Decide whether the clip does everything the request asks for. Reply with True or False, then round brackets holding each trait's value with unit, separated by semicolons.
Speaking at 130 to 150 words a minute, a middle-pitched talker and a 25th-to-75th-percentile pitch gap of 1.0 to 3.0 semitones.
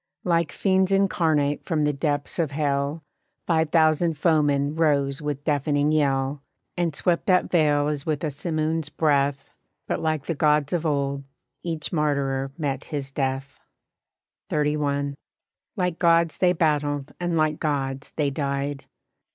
True (140 wpm; 150 Hz; 2.4 semitones)